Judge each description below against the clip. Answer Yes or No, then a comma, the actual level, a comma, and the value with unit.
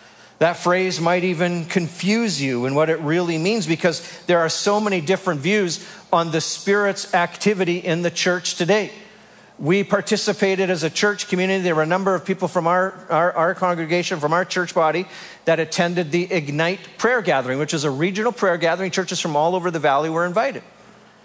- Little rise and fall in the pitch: Yes, narrow, 2.3 semitones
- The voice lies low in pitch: No, medium, 180 Hz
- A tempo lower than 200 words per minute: Yes, average, 190 wpm